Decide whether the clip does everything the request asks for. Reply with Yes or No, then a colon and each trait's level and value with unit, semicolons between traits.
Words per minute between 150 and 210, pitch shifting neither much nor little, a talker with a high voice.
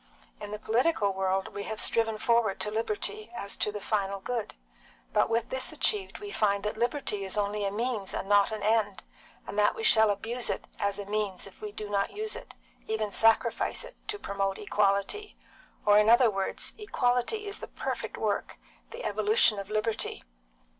Yes: average, 190 wpm; average, 3.0 semitones; high, 215 Hz